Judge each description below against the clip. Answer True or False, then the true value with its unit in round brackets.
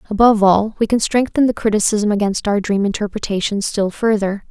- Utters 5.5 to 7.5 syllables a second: True (5.7 syllables/s)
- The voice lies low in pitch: False (210 Hz)